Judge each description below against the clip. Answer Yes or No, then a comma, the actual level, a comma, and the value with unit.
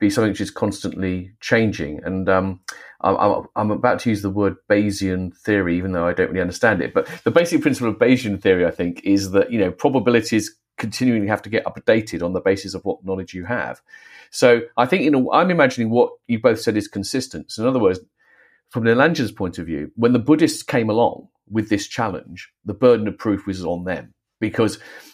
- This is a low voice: Yes, low, 105 Hz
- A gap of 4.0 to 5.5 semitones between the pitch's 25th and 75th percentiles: No, average, 3.6 semitones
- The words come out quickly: Yes, fast, 215 wpm